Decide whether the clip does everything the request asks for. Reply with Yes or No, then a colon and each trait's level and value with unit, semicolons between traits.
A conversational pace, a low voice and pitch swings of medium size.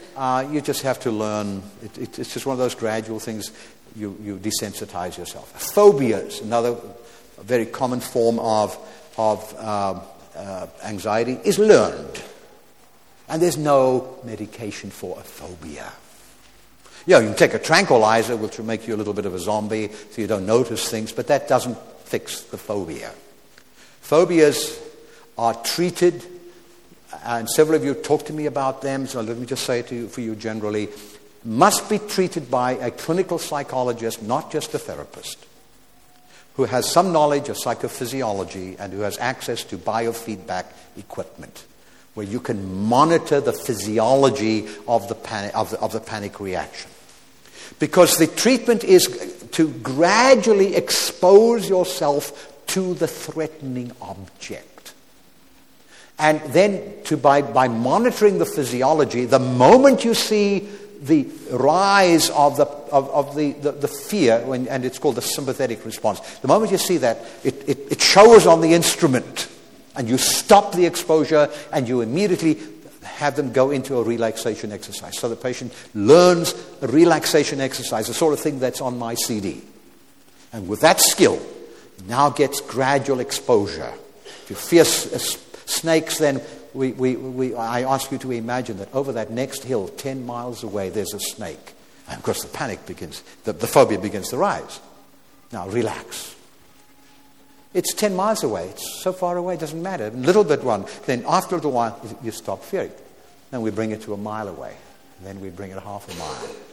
No: average, 165 wpm; low, 130 Hz; wide, 6.1 semitones